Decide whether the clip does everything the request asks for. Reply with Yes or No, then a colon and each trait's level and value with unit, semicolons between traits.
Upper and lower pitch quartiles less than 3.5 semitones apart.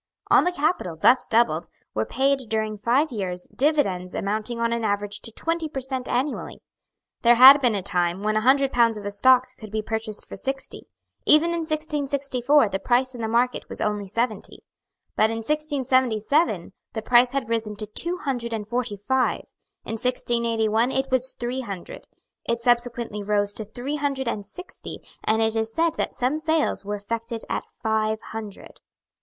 No: average, 3.8 semitones